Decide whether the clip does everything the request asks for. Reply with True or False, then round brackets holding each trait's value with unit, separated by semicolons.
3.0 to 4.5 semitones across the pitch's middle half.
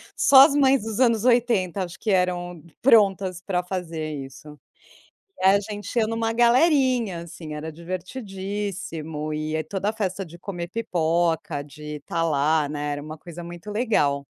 False (5.2 semitones)